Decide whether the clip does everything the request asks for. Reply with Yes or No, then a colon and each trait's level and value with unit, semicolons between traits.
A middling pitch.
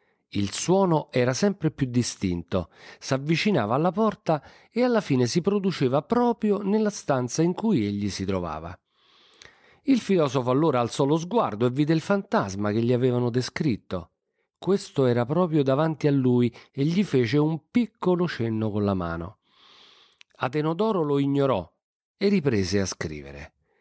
Yes: medium, 145 Hz